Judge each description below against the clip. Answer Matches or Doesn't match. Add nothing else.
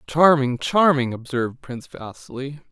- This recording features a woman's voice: Doesn't match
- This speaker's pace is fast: Doesn't match